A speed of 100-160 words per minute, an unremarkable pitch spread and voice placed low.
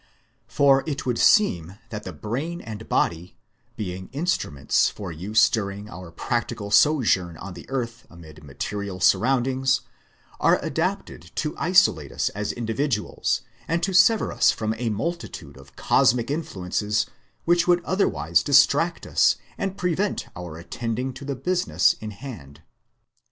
No: average, 140 wpm; wide, 7.8 semitones; low, 115 Hz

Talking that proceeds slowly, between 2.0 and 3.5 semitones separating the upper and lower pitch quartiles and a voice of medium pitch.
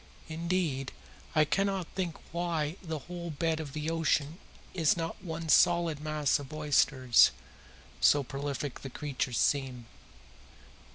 Yes: slow, 125 wpm; average, 2.9 semitones; medium, 155 Hz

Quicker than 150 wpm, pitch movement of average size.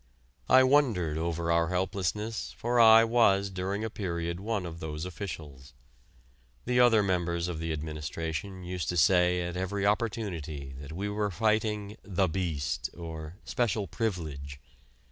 No: average, 145 wpm; average, 4.3 semitones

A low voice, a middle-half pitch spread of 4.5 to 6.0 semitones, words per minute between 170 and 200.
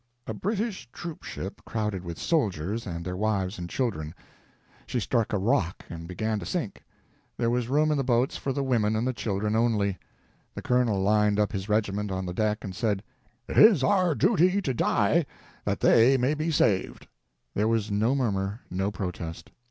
Yes: low, 110 Hz; average, 4.9 semitones; average, 185 wpm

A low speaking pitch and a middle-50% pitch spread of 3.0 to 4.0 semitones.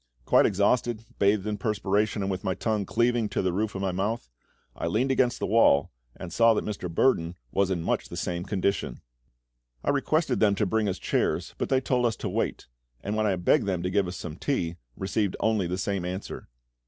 Yes: low, 100 Hz; average, 3.3 semitones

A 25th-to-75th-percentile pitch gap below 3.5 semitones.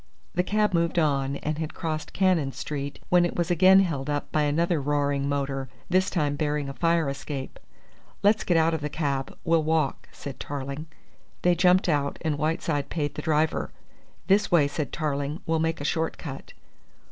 Yes: average, 2.9 semitones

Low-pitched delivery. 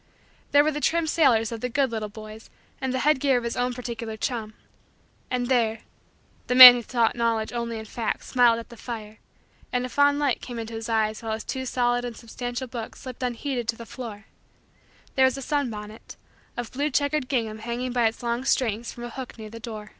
No: high, 240 Hz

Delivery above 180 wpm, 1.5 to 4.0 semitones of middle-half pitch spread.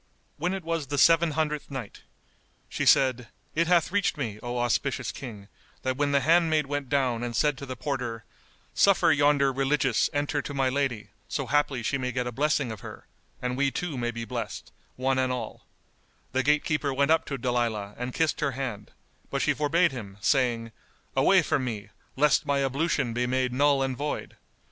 Yes: average, 190 wpm; average, 3.1 semitones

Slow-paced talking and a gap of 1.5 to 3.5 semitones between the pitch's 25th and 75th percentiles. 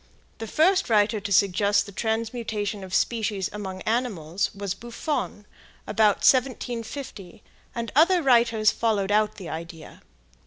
Yes: slow, 125 wpm; average, 2.9 semitones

